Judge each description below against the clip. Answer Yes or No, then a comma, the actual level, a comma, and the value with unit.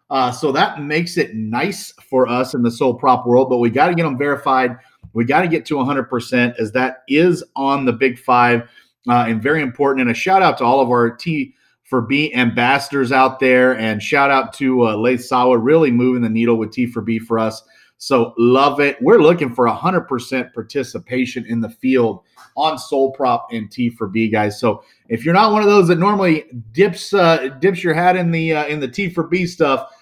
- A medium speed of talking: No, fast, 220 wpm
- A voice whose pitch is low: Yes, low, 130 Hz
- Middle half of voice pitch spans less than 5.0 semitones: Yes, average, 4.6 semitones